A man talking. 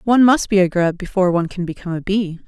No: female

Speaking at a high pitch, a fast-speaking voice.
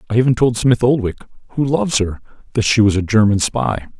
No: low, 115 Hz; fast, 210 wpm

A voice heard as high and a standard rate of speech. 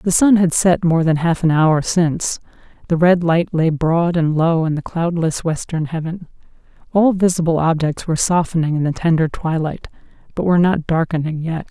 No: medium, 165 Hz; average, 185 wpm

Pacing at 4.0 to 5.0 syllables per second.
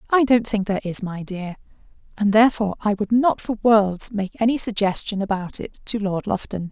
No: 5.3 syllables/s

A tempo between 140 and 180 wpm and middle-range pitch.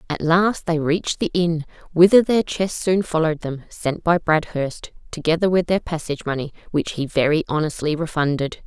Yes: average, 175 wpm; medium, 165 Hz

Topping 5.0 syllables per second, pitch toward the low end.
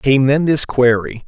No: 4.1 syllables/s; low, 130 Hz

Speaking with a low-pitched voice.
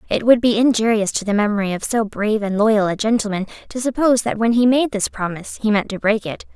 No: high, 215 Hz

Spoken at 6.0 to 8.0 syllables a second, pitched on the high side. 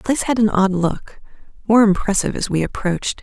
Yes: 6.3 syllables/s; high, 200 Hz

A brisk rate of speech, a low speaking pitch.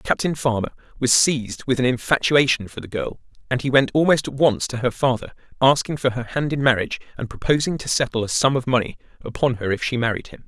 Yes: fast, 225 wpm; low, 130 Hz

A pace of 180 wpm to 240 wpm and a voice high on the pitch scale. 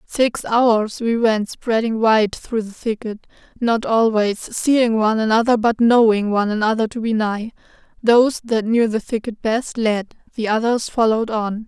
No: average, 165 wpm; high, 225 Hz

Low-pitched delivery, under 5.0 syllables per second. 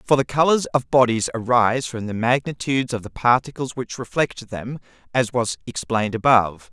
No: low, 125 Hz; 5.4 syllables/s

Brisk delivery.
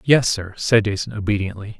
No: average, 170 wpm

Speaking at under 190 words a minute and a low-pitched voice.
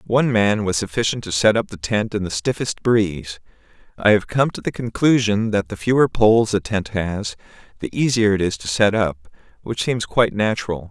No: fast, 205 wpm; low, 105 Hz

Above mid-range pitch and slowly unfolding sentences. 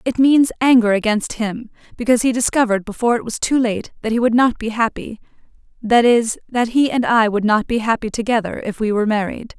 No: high, 230 Hz; fast, 205 wpm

